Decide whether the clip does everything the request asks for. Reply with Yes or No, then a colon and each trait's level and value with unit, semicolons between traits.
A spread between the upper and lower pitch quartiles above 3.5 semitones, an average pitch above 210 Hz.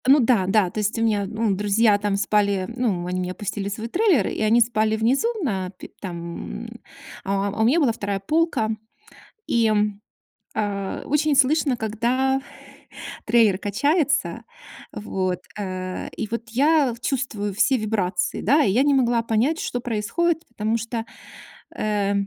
Yes: average, 4.2 semitones; high, 220 Hz